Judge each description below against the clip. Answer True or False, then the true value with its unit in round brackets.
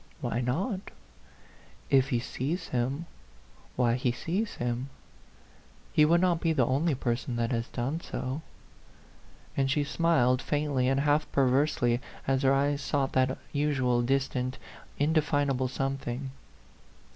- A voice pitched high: False (135 Hz)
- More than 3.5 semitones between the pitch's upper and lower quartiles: False (2.8 semitones)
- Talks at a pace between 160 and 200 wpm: False (135 wpm)